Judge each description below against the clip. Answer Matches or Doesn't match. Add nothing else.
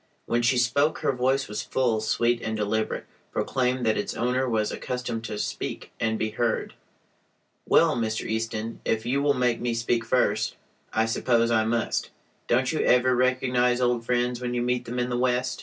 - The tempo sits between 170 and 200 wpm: Matches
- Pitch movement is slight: Matches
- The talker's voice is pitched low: Matches